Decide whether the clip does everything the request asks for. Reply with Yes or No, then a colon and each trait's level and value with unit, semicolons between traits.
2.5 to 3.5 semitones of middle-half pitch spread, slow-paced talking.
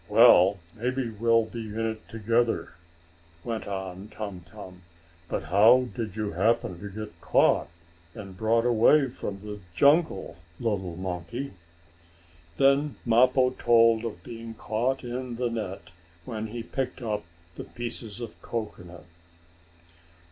Yes: average, 3.0 semitones; slow, 130 wpm